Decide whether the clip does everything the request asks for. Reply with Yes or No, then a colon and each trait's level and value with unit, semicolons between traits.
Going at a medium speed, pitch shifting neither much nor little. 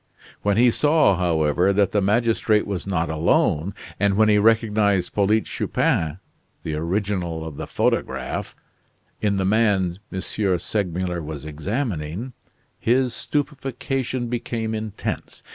No: slow, 125 wpm; average, 4.3 semitones